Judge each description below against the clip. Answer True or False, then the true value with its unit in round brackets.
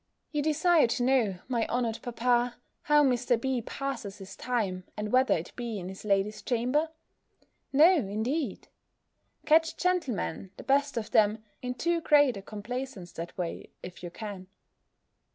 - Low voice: False (245 Hz)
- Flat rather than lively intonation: False (5.1 semitones)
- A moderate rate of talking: True (150 wpm)